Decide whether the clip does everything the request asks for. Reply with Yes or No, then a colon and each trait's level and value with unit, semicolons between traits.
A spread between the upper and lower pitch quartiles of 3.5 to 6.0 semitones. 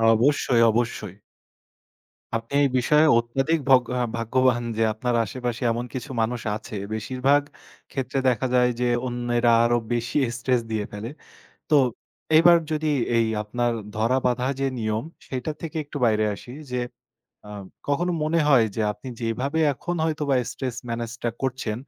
No: average, 2.9 semitones